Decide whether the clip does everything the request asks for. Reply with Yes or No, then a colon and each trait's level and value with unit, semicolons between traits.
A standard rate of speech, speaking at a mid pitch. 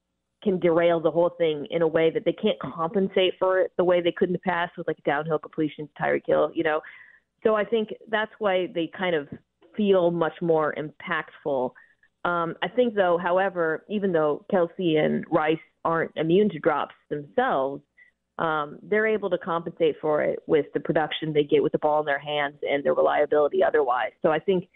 Yes: average, 195 wpm; medium, 170 Hz